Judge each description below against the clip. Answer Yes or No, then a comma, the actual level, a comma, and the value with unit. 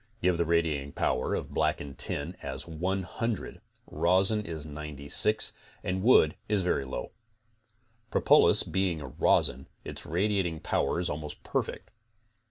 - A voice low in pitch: Yes, very low, 85 Hz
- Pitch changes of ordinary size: Yes, average, 4.0 semitones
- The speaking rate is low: Yes, slow, 130 wpm